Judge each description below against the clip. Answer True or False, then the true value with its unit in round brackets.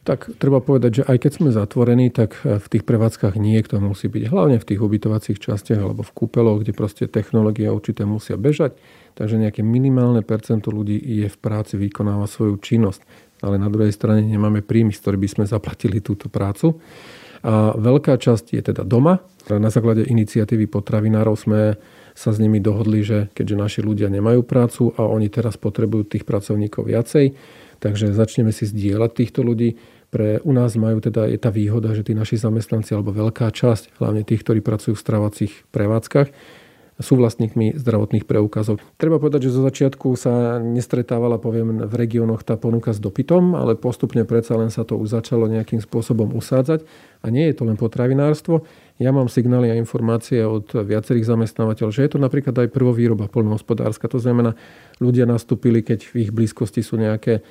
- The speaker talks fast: True (175 wpm)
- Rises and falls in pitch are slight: True (2.2 semitones)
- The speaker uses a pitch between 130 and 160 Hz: False (115 Hz)